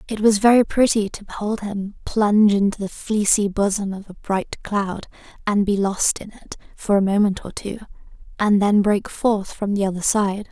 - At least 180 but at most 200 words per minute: Yes, average, 195 wpm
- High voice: Yes, high, 205 Hz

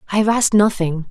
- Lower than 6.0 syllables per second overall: No, 7.1 syllables/s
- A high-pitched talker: Yes, high, 200 Hz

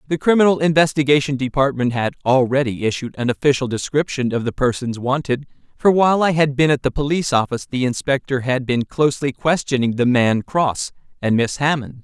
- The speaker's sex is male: Yes, male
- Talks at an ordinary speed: Yes, average, 175 wpm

